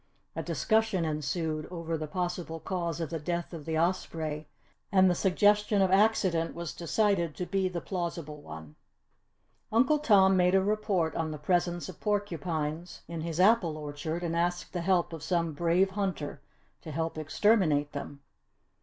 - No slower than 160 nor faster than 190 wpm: Yes, average, 165 wpm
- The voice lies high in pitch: No, medium, 170 Hz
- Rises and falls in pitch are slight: No, average, 3.2 semitones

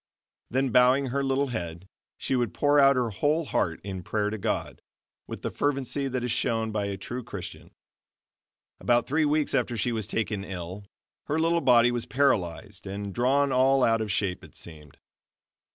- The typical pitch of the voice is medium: No, low, 120 Hz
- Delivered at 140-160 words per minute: No, average, 180 wpm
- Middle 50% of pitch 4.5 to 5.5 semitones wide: Yes, average, 5.0 semitones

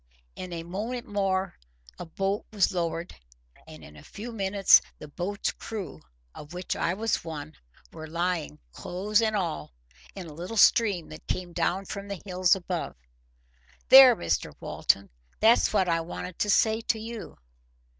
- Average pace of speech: Yes, average, 155 wpm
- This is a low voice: No, medium, 185 Hz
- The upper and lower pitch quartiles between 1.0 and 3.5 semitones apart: No, average, 4.1 semitones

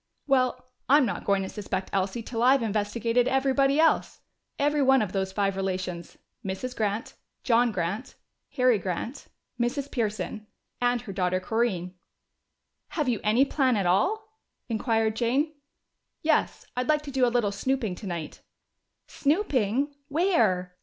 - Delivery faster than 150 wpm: No, average, 140 wpm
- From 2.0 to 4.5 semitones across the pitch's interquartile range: No, average, 5.3 semitones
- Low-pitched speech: No, high, 230 Hz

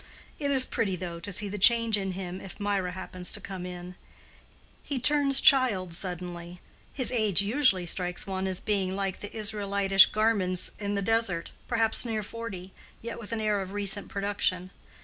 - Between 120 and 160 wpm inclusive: No, average, 170 wpm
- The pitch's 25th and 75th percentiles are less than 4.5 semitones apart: Yes, average, 3.3 semitones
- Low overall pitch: No, high, 200 Hz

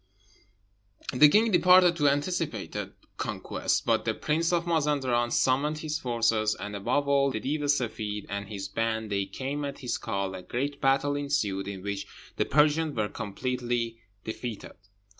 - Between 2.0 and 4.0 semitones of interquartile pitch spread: No, average, 5.3 semitones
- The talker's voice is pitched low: Yes, low, 130 Hz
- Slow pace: No, average, 160 wpm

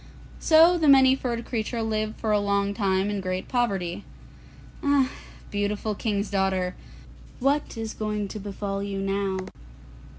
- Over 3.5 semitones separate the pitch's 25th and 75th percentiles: No, average, 3.2 semitones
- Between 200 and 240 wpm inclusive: No, average, 140 wpm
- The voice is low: No, high, 210 Hz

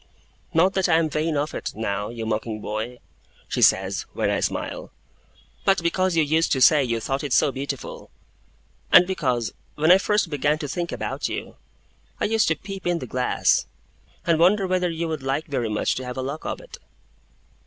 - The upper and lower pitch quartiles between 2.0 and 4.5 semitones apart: No, wide, 5.4 semitones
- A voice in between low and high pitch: Yes, medium, 155 Hz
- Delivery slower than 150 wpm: No, average, 195 wpm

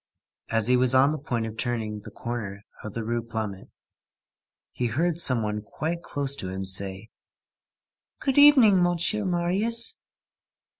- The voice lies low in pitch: Yes, low, 120 Hz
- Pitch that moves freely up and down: Yes, wide, 8.1 semitones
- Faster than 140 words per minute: Yes, average, 150 wpm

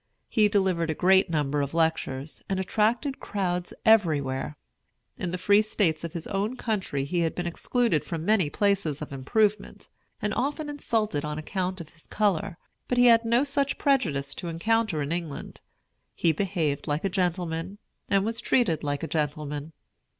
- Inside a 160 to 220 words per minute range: Yes, average, 170 wpm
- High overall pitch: No, medium, 180 Hz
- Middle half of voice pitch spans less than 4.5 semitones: No, wide, 5.4 semitones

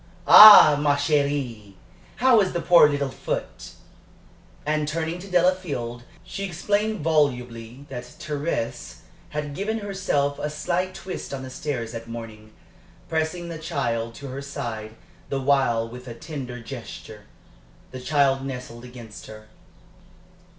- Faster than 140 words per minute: No, slow, 135 wpm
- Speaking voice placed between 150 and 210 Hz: No, medium, 140 Hz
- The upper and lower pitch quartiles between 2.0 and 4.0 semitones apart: No, average, 5.2 semitones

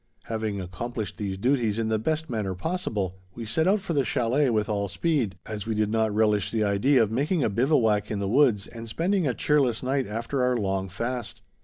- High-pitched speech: No, low, 115 Hz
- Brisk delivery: Yes, fast, 210 wpm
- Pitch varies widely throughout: No, average, 4.4 semitones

